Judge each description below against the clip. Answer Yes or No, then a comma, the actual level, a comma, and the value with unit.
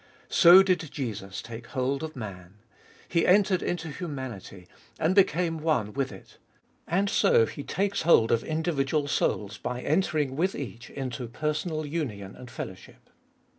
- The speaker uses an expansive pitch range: Yes, wide, 6.2 semitones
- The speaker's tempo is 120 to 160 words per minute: Yes, average, 145 wpm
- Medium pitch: Yes, medium, 145 Hz